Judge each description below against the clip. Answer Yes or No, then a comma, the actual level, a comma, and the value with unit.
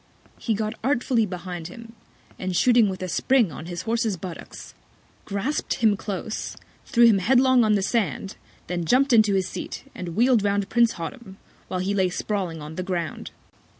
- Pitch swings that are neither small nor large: Yes, average, 4.2 semitones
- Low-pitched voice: No, high, 200 Hz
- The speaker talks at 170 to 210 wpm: Yes, average, 175 wpm